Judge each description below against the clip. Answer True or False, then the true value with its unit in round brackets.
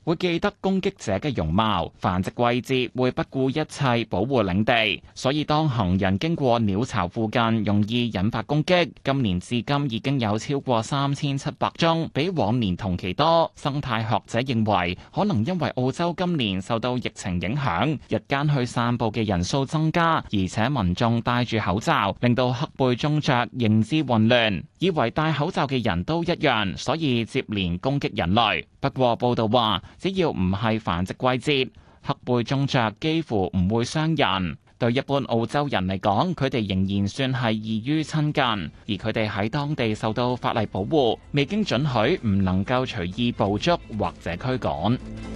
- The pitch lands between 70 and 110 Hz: False (120 Hz)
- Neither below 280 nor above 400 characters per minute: False (255 characters per minute)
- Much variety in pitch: False (5.0 semitones)